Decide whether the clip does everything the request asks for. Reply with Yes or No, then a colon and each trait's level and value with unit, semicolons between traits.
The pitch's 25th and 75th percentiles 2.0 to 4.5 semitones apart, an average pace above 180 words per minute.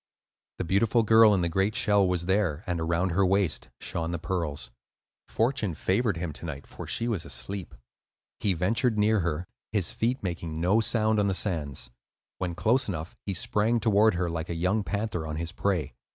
Yes: average, 4.2 semitones; average, 190 wpm